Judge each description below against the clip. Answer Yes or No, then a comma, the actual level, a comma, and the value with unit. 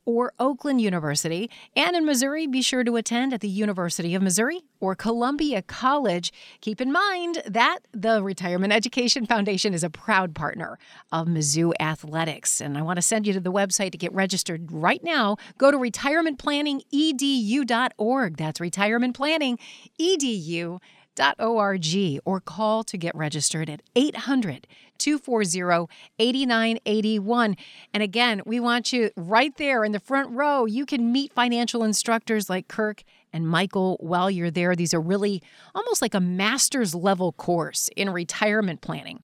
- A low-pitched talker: No, high, 215 Hz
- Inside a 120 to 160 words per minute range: Yes, average, 145 wpm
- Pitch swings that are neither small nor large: No, wide, 5.7 semitones